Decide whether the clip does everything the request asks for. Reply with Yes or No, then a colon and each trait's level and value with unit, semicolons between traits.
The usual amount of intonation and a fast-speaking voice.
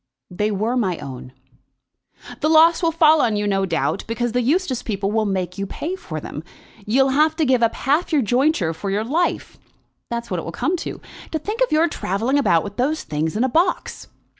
No: wide, 7.9 semitones; fast, 215 wpm